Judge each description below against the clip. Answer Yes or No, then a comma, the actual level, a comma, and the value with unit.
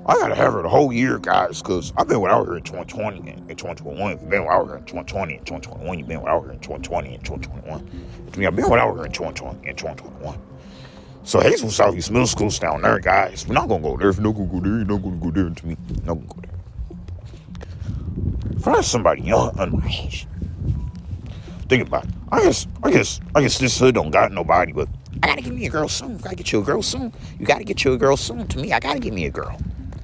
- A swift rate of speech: Yes, fast, 275 wpm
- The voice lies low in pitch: Yes, very low, 90 Hz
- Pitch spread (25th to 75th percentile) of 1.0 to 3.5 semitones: No, average, 5.0 semitones